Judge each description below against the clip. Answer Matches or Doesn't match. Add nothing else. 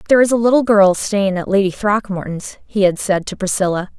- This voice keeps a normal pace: Doesn't match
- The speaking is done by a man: Doesn't match